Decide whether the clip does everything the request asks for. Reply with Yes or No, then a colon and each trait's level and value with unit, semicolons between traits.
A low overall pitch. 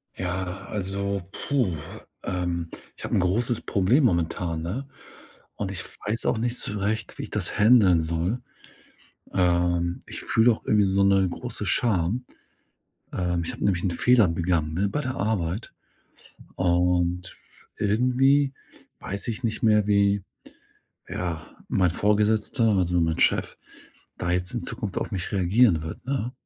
Yes: low, 100 Hz